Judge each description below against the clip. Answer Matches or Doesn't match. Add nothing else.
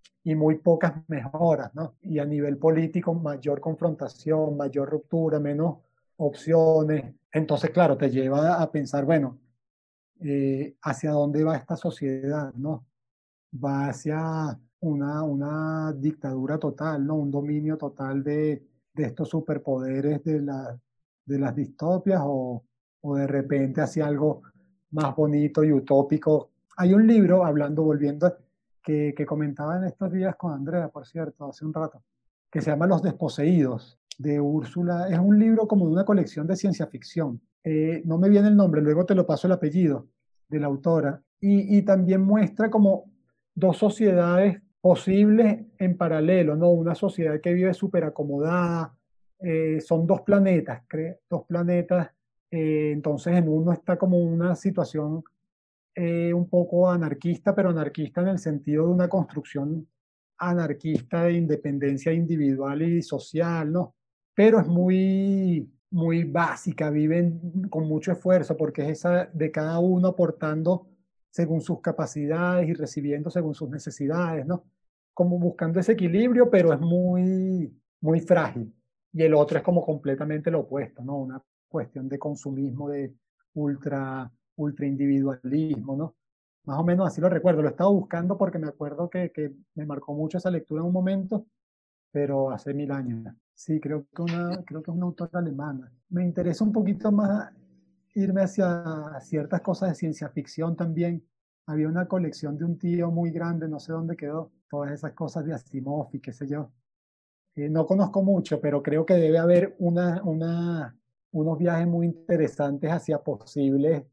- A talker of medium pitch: Matches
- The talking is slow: Doesn't match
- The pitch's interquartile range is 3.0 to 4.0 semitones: Matches